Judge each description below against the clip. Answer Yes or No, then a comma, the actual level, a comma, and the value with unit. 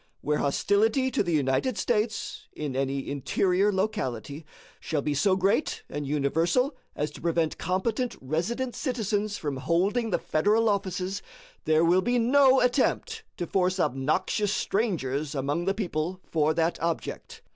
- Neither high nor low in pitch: Yes, medium, 180 Hz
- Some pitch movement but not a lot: No, wide, 6.1 semitones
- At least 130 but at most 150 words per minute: Yes, average, 145 wpm